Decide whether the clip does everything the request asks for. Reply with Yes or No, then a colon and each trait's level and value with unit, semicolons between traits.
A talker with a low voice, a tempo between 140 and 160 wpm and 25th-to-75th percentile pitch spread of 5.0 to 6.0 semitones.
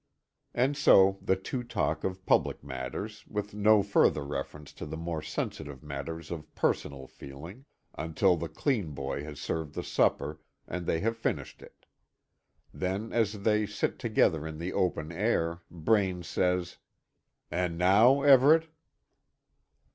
Yes: very low, 90 Hz; average, 145 wpm; wide, 5.4 semitones